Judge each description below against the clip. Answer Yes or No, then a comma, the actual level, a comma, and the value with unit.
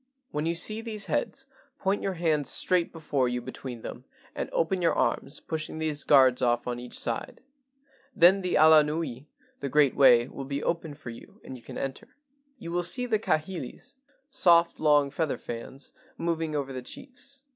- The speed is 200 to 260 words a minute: No, average, 175 wpm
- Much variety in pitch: No, average, 4.5 semitones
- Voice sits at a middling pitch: Yes, medium, 155 Hz